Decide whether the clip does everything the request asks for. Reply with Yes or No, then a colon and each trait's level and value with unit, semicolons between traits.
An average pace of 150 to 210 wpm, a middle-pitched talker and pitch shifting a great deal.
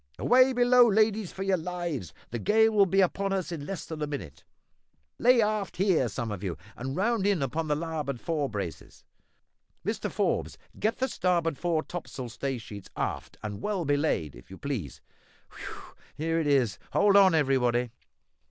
Yes: average, 175 wpm; medium, 165 Hz; wide, 7.2 semitones